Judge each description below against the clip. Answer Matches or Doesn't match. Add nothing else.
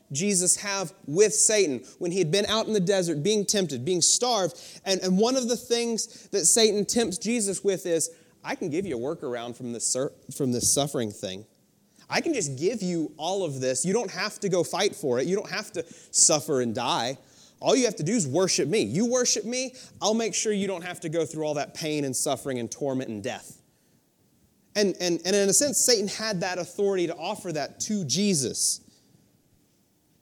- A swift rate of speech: Matches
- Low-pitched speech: Doesn't match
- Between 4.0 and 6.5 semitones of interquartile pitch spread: Matches